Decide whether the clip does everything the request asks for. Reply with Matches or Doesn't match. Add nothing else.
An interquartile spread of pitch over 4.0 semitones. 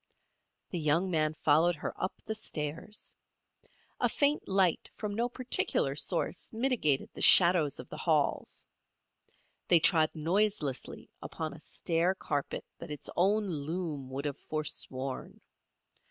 Matches